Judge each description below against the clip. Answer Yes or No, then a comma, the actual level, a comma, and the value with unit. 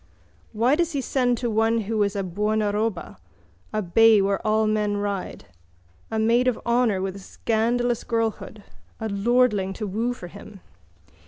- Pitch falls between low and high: No, high, 220 Hz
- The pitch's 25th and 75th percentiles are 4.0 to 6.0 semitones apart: No, narrow, 2.6 semitones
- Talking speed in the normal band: Yes, average, 160 wpm